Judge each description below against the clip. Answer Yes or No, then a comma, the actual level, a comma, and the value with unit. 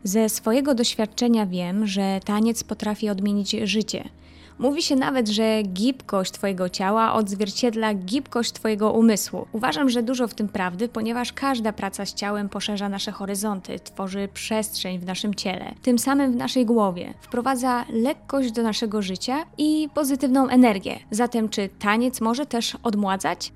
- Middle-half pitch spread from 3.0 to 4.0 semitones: Yes, average, 3.3 semitones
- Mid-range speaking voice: No, high, 220 Hz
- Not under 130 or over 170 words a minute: Yes, average, 150 wpm